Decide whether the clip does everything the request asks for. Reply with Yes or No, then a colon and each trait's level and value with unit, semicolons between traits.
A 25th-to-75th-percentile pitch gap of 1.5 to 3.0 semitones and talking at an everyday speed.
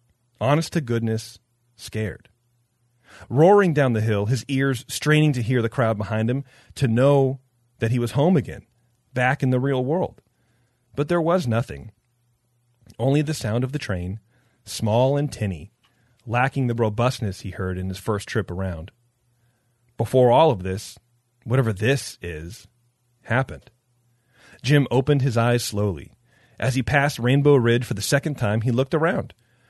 Yes: average, 2.7 semitones; average, 155 wpm